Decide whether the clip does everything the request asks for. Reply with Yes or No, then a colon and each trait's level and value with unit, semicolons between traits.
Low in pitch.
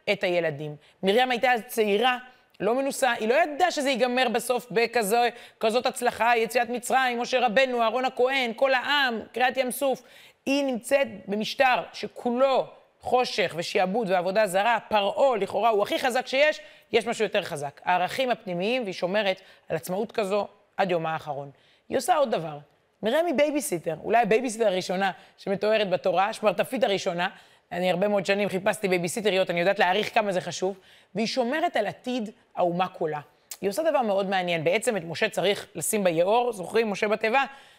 No: high, 220 Hz